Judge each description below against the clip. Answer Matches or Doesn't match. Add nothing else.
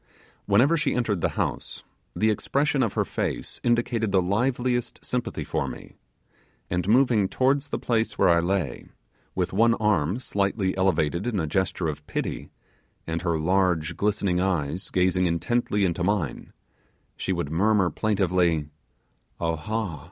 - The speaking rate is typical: Matches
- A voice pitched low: Matches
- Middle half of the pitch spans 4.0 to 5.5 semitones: Matches